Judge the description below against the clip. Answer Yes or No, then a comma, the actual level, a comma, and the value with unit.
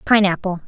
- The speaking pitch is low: No, high, 190 Hz